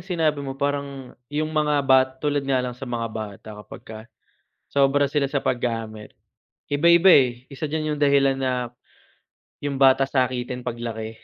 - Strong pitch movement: No, average, 2.8 semitones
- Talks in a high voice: No, low, 135 Hz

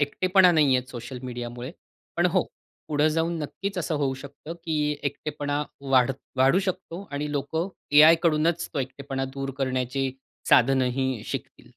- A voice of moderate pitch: Yes, medium, 145 Hz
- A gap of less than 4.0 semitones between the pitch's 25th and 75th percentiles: Yes, average, 3.6 semitones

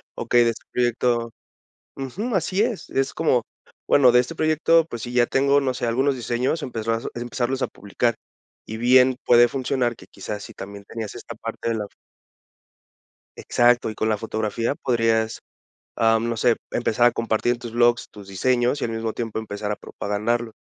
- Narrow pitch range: Yes, narrow, 2.3 semitones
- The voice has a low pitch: Yes, low, 120 Hz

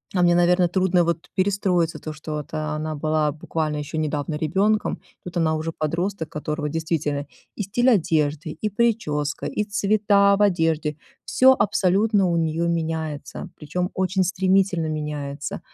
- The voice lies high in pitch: No, medium, 165 Hz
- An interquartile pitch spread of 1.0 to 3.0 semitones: No, average, 3.7 semitones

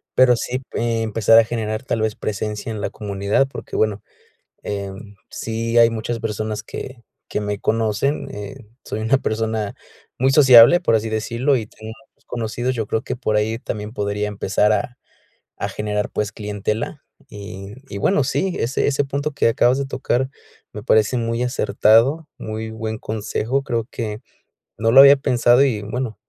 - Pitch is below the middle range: Yes, low, 110 Hz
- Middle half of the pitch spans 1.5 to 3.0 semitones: Yes, average, 2.7 semitones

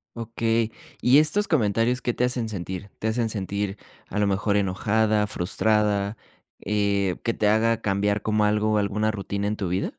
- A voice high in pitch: No, low, 105 Hz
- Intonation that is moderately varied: No, narrow, 2.0 semitones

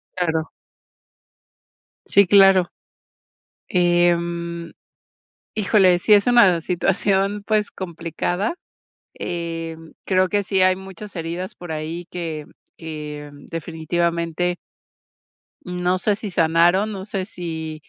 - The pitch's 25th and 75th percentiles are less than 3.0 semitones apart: Yes, narrow, 2.5 semitones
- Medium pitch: Yes, medium, 175 Hz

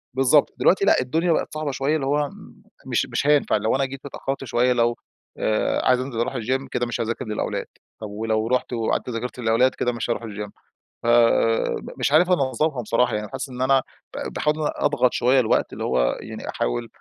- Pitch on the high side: No, low, 125 Hz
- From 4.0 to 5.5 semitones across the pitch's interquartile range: No, average, 3.1 semitones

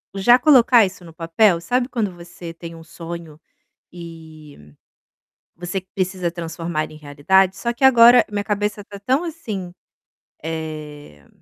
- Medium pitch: Yes, medium, 175 Hz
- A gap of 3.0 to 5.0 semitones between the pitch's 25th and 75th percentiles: Yes, average, 4.3 semitones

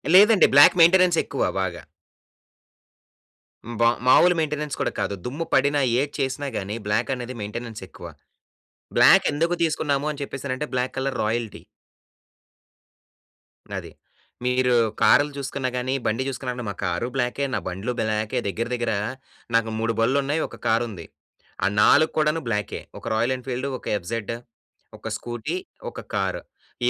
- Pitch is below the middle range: Yes, low, 125 Hz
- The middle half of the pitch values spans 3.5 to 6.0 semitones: Yes, average, 4.0 semitones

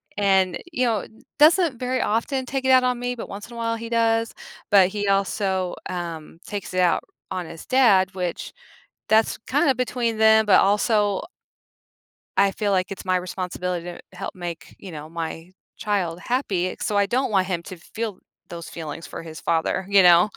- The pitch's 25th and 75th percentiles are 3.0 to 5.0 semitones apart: Yes, average, 4.2 semitones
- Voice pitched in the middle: No, high, 200 Hz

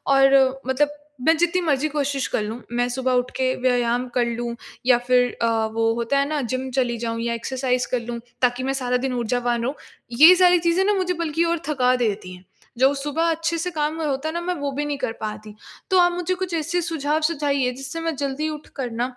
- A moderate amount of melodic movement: Yes, average, 4.3 semitones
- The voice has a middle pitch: No, very high, 270 Hz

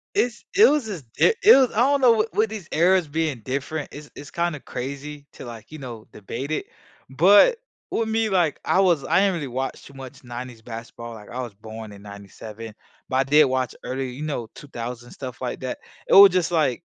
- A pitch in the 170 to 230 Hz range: No, medium, 140 Hz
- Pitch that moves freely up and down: Yes, wide, 6.8 semitones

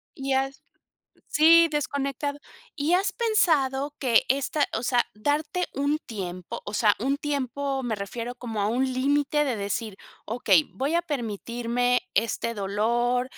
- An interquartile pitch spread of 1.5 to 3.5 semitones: No, average, 4.0 semitones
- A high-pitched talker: Yes, very high, 260 Hz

